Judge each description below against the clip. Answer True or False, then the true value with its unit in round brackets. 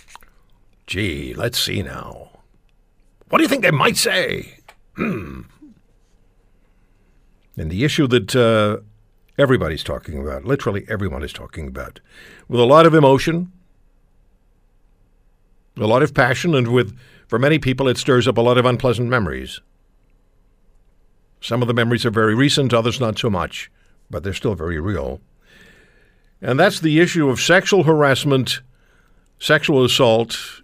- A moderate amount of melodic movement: False (5.8 semitones)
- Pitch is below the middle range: True (120 Hz)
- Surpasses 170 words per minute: False (135 wpm)